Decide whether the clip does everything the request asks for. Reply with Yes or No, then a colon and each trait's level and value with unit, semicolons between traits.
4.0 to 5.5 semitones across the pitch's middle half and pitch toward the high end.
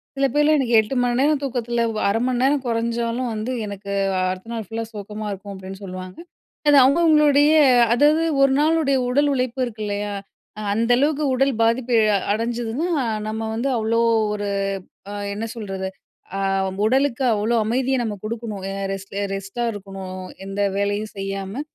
Yes: average, 4.5 semitones; high, 230 Hz